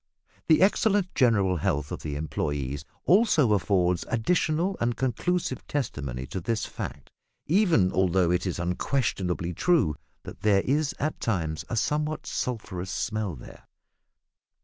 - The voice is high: No, low, 105 Hz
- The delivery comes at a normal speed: No, slow, 130 wpm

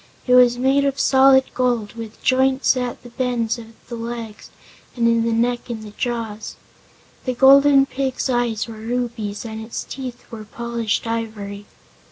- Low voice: No, high, 235 Hz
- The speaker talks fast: No, average, 160 wpm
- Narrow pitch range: Yes, narrow, 2.2 semitones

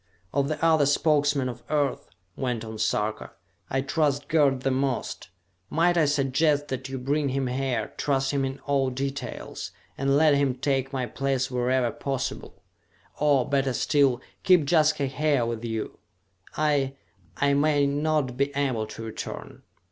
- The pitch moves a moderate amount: No, narrow, 2.0 semitones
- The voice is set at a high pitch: No, low, 135 Hz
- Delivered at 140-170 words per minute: Yes, average, 155 wpm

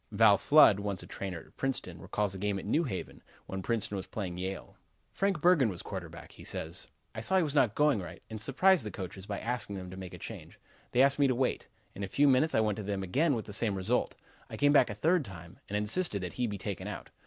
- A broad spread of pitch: Yes, wide, 5.8 semitones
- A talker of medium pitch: No, low, 105 Hz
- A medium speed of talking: No, fast, 255 wpm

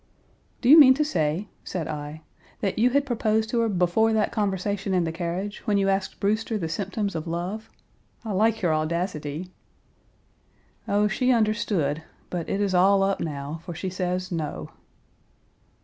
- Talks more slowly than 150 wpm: No, average, 165 wpm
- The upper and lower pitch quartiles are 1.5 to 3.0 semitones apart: No, average, 4.2 semitones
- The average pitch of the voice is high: Yes, high, 195 Hz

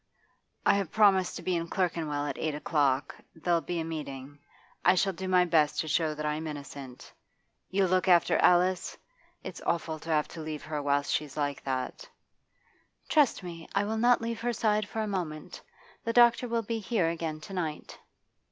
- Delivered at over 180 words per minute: Yes, average, 190 wpm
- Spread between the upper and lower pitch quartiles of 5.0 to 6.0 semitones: No, average, 4.5 semitones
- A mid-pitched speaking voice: Yes, medium, 170 Hz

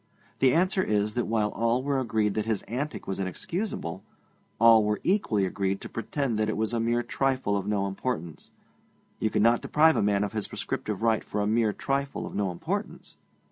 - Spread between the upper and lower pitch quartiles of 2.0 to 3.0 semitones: No, average, 3.7 semitones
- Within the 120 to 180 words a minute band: No, average, 195 wpm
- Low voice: Yes, low, 110 Hz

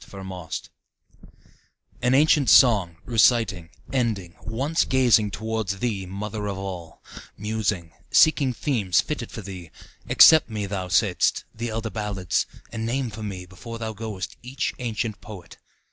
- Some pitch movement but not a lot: Yes, average, 3.6 semitones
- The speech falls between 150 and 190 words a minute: No, average, 140 wpm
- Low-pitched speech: Yes, low, 110 Hz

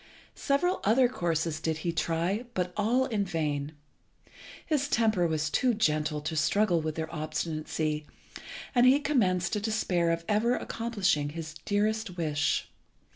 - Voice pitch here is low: No, medium, 175 Hz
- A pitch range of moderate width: No, wide, 5.8 semitones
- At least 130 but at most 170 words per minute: Yes, average, 140 wpm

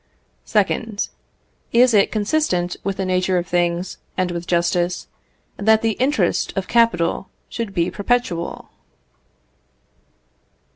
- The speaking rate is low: Yes, slow, 110 wpm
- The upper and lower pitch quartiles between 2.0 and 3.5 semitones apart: No, average, 4.0 semitones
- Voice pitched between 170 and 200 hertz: Yes, high, 190 Hz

